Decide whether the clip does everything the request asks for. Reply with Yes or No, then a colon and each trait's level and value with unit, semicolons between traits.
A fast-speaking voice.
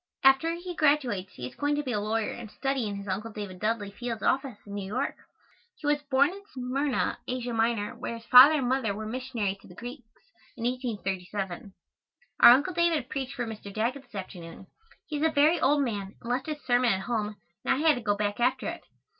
Yes: fast, 220 wpm